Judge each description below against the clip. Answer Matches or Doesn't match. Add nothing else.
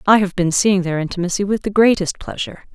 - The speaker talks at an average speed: Doesn't match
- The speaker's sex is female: Matches